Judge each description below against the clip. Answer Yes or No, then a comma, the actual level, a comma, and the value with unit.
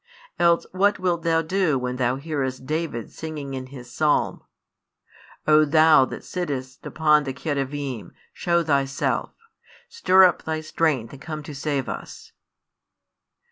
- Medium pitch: Yes, medium, 150 Hz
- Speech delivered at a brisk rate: No, average, 140 wpm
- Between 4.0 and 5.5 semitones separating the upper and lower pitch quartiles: No, average, 3.5 semitones